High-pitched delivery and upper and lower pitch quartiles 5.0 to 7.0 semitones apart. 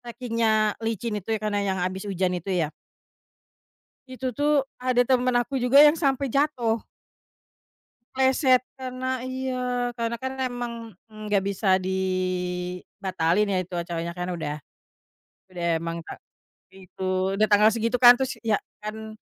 Yes: high, 220 Hz; average, 5.3 semitones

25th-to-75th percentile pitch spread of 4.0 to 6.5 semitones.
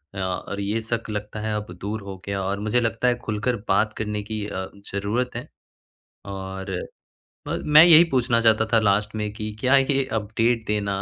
No: narrow, 2.5 semitones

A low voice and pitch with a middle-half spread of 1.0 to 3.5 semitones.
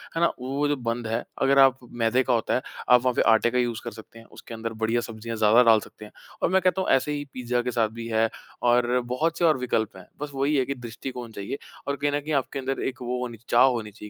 Yes: low, 125 Hz; average, 2.9 semitones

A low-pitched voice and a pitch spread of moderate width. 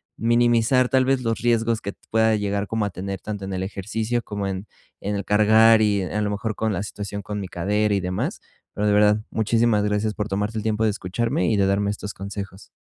No: low, 105 Hz; narrow, 1.9 semitones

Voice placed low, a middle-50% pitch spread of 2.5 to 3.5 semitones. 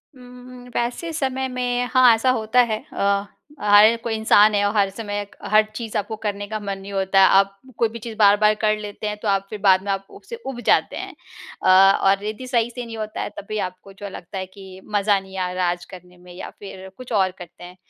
No: high, 205 Hz; average, 2.8 semitones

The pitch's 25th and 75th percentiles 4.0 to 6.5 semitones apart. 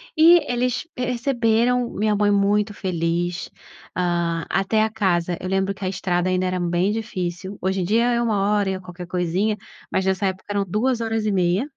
No: average, 3.5 semitones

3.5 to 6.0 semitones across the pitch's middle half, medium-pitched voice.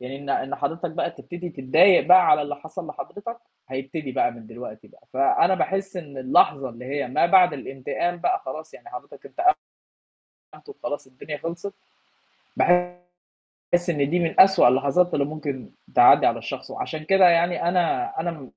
Yes: average, 4.6 semitones; medium, 160 Hz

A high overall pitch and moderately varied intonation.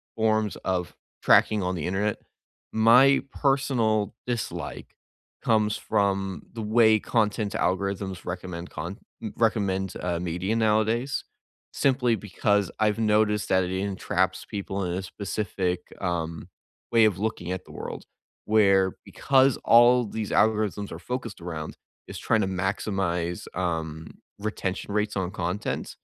No: low, 100 Hz; average, 3.0 semitones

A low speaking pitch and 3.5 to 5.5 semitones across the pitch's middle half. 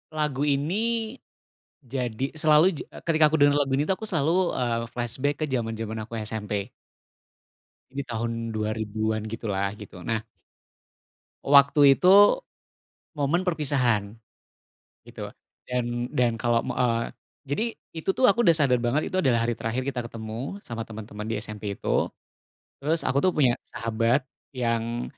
Yes: low, 120 Hz; average, 4.2 semitones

